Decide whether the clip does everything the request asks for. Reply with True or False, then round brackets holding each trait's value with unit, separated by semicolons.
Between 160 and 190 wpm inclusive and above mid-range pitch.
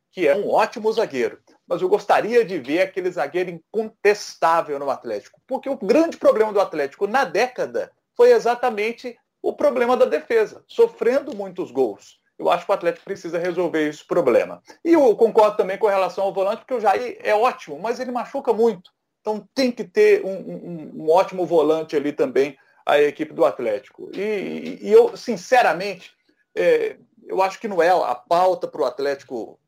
True (180 wpm; 225 Hz)